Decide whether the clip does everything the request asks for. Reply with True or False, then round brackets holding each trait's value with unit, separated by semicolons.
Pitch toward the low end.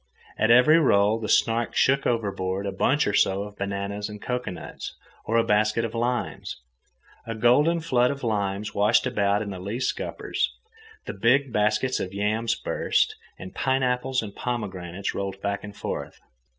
True (110 Hz)